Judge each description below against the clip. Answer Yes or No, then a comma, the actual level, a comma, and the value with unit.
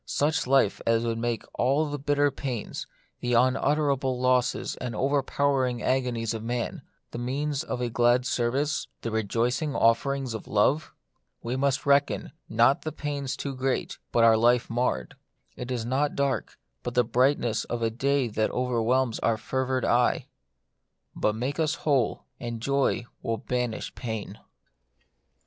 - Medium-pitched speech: No, low, 125 Hz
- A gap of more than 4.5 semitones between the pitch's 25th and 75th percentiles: No, average, 3.0 semitones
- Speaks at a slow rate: No, average, 155 wpm